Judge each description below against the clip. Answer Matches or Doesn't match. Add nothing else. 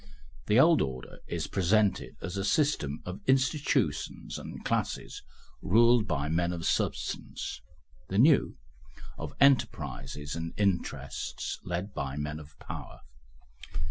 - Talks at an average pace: Doesn't match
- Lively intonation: Matches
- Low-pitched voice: Matches